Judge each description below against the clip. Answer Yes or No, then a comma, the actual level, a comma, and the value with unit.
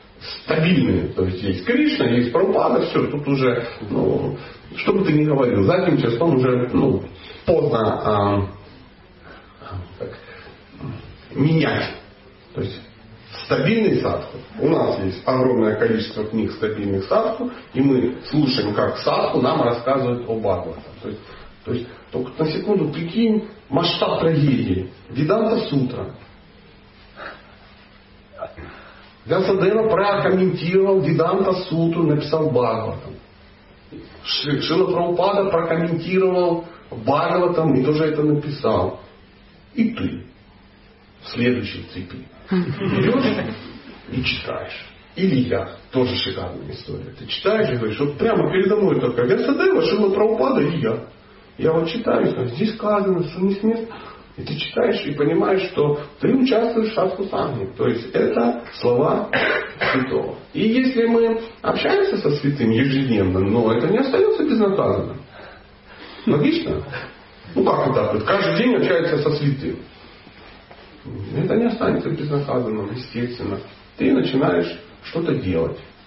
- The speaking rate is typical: Yes, average, 120 wpm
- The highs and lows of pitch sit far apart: Yes, wide, 8.6 semitones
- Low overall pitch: No, medium, 145 Hz